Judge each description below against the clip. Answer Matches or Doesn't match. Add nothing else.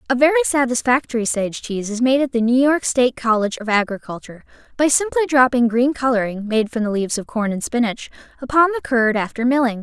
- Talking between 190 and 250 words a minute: Matches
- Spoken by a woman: Matches